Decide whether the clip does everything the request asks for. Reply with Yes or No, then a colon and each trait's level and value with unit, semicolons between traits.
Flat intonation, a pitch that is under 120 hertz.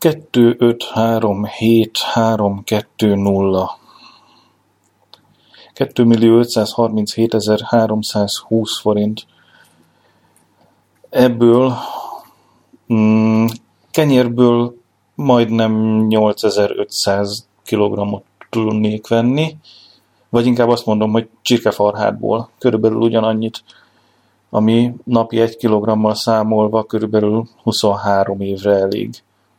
Yes: narrow, 2.1 semitones; low, 110 Hz